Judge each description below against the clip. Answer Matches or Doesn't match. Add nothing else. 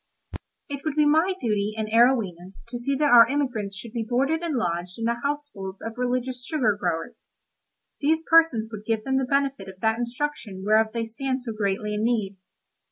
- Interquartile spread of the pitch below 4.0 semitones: Doesn't match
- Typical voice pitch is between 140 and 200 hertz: Doesn't match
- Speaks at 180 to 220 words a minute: Matches